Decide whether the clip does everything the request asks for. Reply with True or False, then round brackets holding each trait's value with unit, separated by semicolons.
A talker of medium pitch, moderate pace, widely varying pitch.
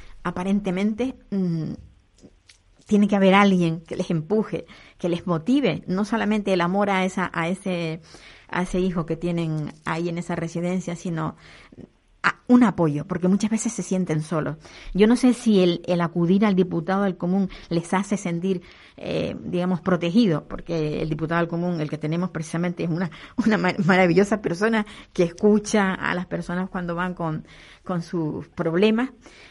False (180 Hz; 165 wpm; 2.9 semitones)